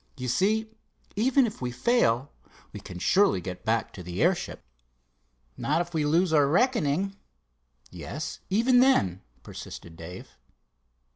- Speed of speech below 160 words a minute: Yes, slow, 135 wpm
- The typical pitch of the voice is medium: Yes, medium, 160 Hz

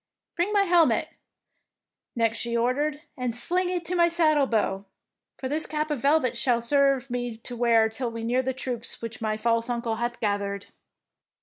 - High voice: Yes, high, 245 Hz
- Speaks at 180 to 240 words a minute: Yes, average, 190 wpm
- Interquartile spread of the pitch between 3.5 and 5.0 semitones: Yes, average, 4.6 semitones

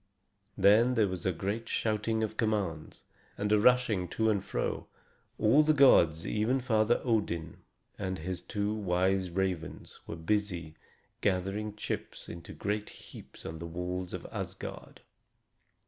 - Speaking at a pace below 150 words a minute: Yes, average, 140 wpm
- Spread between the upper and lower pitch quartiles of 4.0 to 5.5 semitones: No, average, 3.3 semitones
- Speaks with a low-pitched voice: Yes, low, 100 Hz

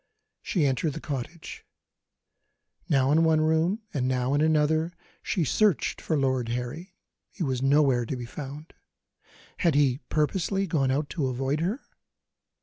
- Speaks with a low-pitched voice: No, medium, 150 Hz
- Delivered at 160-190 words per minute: No, average, 145 wpm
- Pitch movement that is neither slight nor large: Yes, average, 3.5 semitones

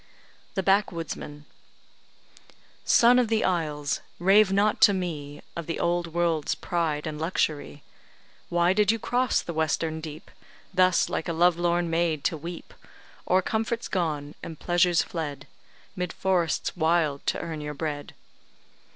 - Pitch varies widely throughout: No, average, 3.0 semitones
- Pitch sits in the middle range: Yes, medium, 170 Hz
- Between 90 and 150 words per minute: Yes, average, 140 wpm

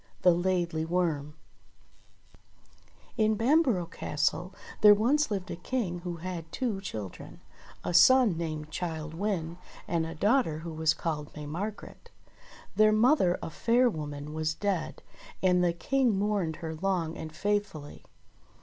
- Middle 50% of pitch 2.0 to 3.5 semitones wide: No, average, 4.6 semitones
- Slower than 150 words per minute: Yes, average, 140 wpm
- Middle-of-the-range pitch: Yes, medium, 175 Hz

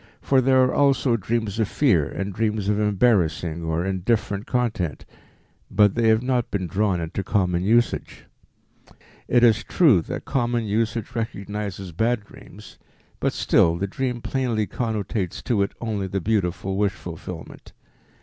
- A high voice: No, low, 105 Hz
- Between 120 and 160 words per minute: Yes, average, 150 wpm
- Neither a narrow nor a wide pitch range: Yes, average, 3.7 semitones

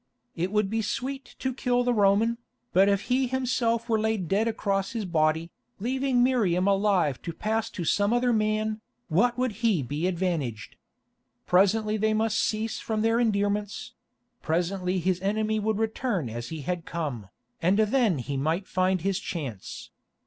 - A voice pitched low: No, high, 205 Hz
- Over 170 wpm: No, average, 165 wpm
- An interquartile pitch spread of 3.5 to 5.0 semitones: Yes, average, 4.0 semitones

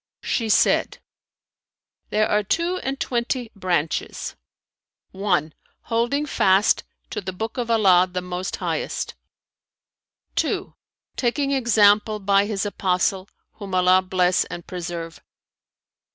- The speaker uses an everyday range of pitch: Yes, average, 3.9 semitones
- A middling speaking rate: No, slow, 110 wpm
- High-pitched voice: Yes, high, 200 Hz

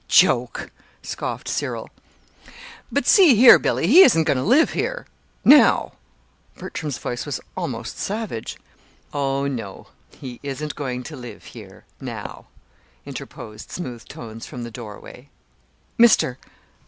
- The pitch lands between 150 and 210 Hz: No, medium, 140 Hz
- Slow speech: Yes, slow, 125 wpm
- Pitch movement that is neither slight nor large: No, wide, 8.7 semitones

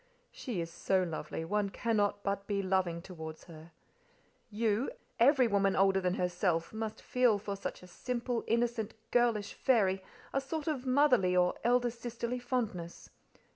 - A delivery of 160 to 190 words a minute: No, average, 145 wpm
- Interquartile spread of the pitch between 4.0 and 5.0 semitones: Yes, average, 4.7 semitones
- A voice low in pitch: No, high, 205 Hz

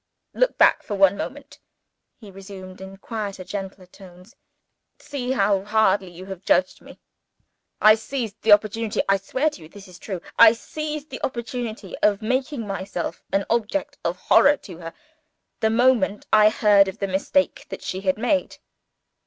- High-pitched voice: Yes, high, 205 Hz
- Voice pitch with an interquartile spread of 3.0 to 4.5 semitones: Yes, average, 3.6 semitones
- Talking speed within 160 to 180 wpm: Yes, average, 170 wpm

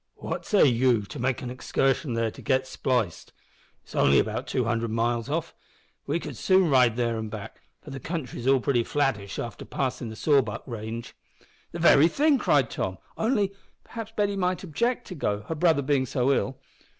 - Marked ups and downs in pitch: Yes, wide, 5.7 semitones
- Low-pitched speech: Yes, low, 130 Hz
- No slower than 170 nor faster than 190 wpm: Yes, average, 185 wpm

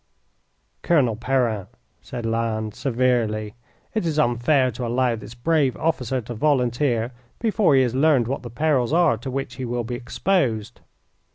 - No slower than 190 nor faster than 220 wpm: No, average, 155 wpm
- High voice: No, low, 125 Hz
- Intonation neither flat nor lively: Yes, average, 3.4 semitones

